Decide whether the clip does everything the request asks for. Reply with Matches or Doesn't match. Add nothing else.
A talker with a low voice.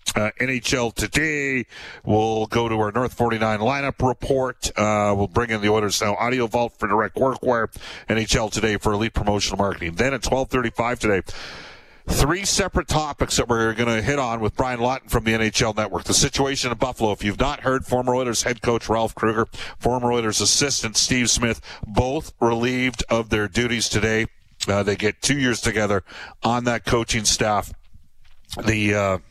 Matches